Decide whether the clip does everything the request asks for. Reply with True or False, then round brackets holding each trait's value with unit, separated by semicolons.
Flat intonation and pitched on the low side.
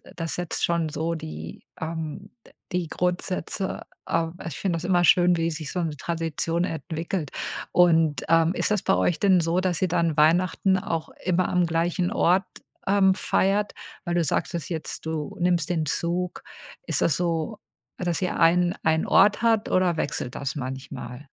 False (2.1 semitones; 170 Hz)